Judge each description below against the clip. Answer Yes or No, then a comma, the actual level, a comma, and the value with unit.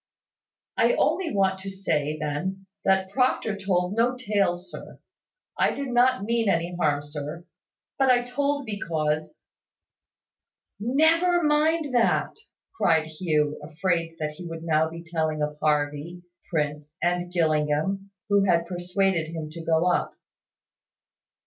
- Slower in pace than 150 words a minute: Yes, slow, 135 wpm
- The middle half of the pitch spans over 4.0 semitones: Yes, average, 4.9 semitones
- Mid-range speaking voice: Yes, medium, 175 Hz